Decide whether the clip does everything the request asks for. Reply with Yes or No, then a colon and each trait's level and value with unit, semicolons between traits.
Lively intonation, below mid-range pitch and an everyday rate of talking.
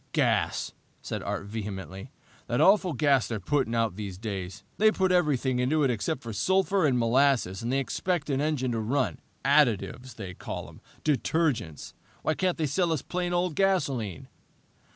Yes: wide, 6.2 semitones; low, 130 Hz; average, 165 wpm